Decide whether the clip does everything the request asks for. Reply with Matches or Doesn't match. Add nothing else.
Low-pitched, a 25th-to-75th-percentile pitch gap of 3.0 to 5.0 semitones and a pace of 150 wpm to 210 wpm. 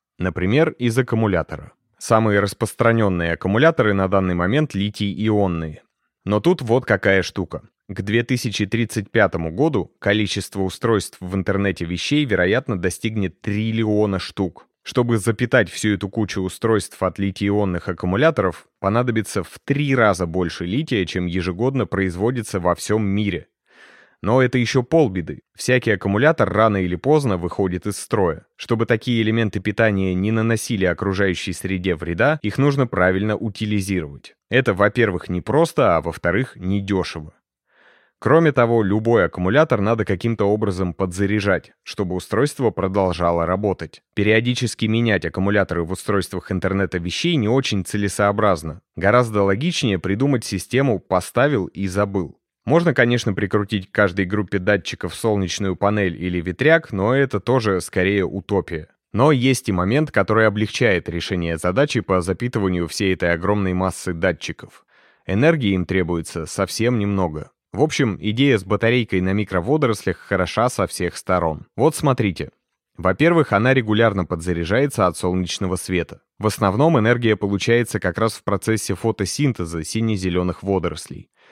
Doesn't match